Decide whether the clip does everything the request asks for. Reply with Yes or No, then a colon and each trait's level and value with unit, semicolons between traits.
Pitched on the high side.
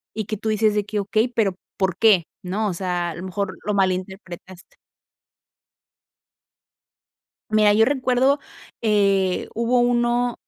Yes: high, 210 Hz